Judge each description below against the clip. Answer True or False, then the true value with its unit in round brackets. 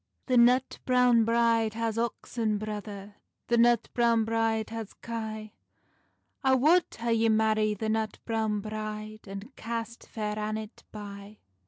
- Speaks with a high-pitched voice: True (220 Hz)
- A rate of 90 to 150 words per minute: True (140 wpm)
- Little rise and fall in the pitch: True (1.5 semitones)